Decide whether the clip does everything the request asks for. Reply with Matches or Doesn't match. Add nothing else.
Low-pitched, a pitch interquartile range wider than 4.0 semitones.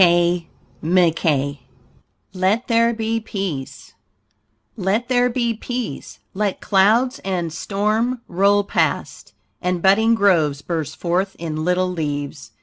Doesn't match